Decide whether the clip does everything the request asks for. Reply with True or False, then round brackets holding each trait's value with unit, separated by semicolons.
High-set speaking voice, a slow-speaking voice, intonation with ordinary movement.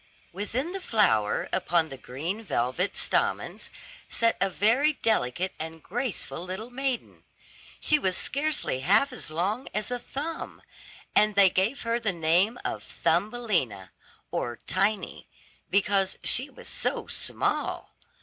False (200 Hz; 130 wpm; 6.0 semitones)